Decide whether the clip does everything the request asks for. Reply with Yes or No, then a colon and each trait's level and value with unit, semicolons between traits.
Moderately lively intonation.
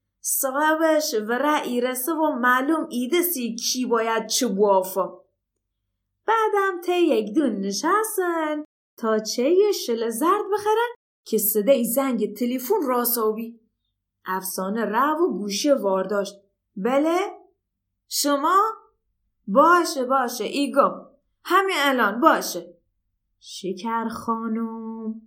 No: wide, 7.1 semitones